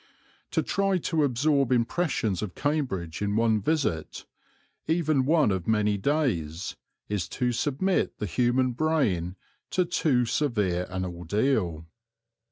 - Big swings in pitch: Yes, wide, 7.8 semitones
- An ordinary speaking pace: No, slow, 125 wpm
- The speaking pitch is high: No, low, 120 Hz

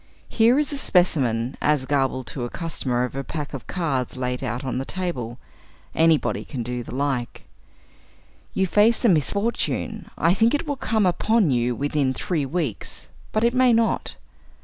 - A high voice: No, medium, 150 Hz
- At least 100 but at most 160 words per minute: No, average, 170 wpm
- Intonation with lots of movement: Yes, wide, 8.3 semitones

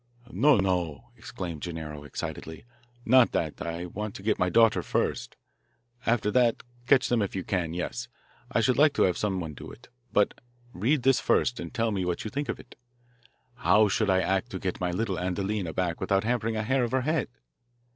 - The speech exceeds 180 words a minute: Yes, average, 195 wpm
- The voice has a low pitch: Yes, low, 100 Hz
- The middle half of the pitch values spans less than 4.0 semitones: No, average, 5.0 semitones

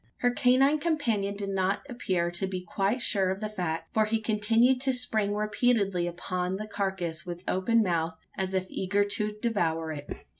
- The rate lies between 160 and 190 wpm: Yes, average, 180 wpm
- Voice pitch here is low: No, high, 200 Hz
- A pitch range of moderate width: Yes, average, 3.7 semitones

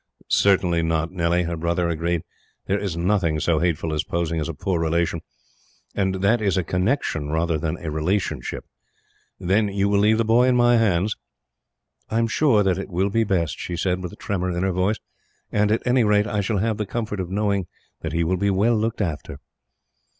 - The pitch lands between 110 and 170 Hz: No, very low, 95 Hz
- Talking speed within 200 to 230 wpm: Yes, fast, 205 wpm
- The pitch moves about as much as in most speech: Yes, average, 3.6 semitones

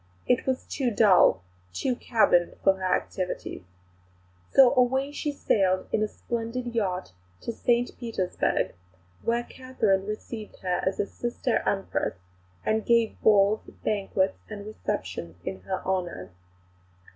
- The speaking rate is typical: No, slow, 130 wpm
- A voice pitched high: Yes, high, 215 Hz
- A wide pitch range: No, average, 4.1 semitones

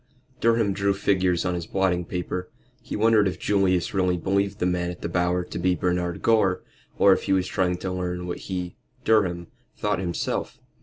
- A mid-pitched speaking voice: No, very low, 90 Hz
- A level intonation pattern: Yes, narrow, 1.7 semitones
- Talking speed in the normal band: Yes, average, 190 wpm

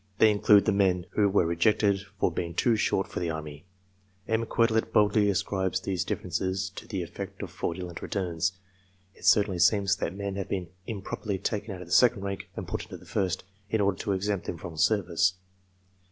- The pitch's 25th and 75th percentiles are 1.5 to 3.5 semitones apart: Yes, narrow, 2.5 semitones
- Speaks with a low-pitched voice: Yes, very low, 95 Hz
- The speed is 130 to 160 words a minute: No, average, 195 wpm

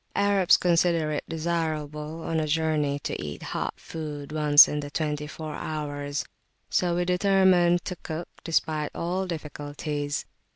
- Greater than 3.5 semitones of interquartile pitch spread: No, narrow, 2.5 semitones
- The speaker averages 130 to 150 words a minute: Yes, average, 140 wpm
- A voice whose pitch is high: No, medium, 155 Hz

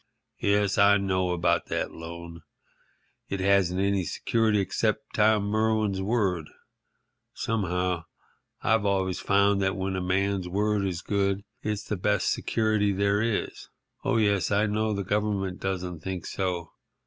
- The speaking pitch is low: Yes, low, 100 Hz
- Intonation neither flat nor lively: No, narrow, 2.0 semitones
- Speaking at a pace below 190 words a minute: Yes, average, 140 wpm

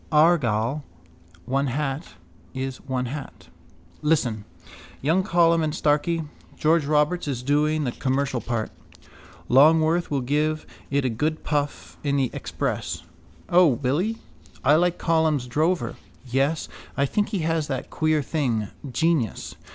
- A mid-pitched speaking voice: Yes, medium, 150 Hz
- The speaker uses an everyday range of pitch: Yes, average, 3.3 semitones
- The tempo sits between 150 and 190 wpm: No, slow, 135 wpm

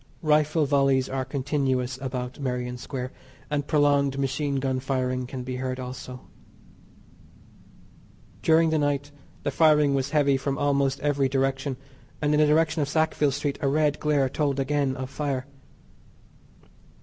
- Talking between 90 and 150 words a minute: Yes, average, 145 wpm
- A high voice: No, medium, 140 Hz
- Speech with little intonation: Yes, narrow, 2.0 semitones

